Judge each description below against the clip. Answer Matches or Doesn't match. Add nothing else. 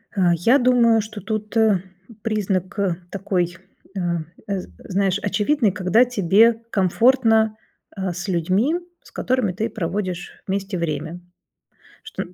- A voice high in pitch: Matches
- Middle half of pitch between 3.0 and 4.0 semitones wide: Matches